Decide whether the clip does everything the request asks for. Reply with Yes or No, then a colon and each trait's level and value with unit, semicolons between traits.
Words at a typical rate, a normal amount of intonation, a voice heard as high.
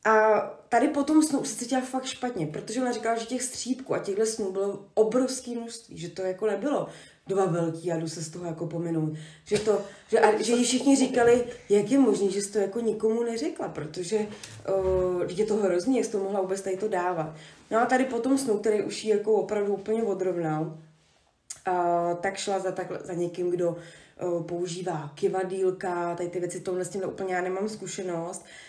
No: fast, 195 wpm; average, 4.1 semitones; high, 200 Hz